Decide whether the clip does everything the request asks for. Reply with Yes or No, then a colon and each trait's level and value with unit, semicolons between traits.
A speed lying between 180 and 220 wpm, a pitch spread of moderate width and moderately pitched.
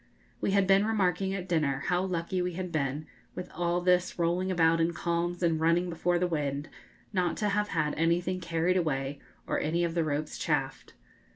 No: average, 190 wpm; narrow, 2.0 semitones; medium, 175 Hz